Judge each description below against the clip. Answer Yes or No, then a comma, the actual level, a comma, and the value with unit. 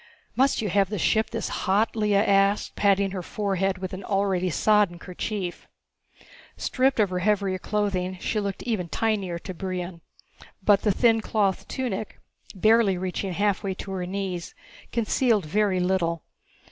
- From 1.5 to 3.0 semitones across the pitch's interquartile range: Yes, narrow, 2.4 semitones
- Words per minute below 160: Yes, average, 150 wpm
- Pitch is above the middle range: Yes, high, 195 Hz